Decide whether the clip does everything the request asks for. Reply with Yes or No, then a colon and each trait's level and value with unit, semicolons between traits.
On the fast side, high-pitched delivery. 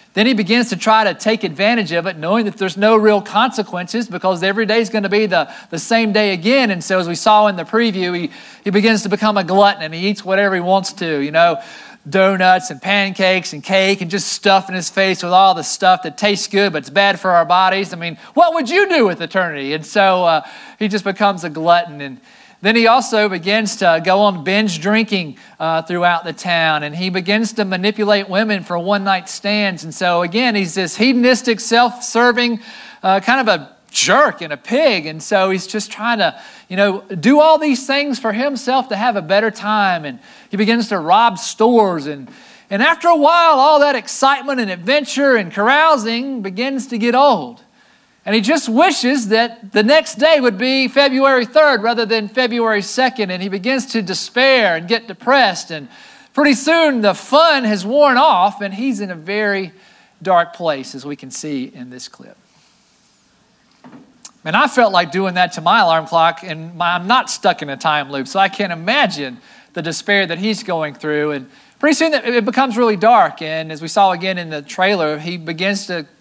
Yes: fast, 210 wpm; high, 205 Hz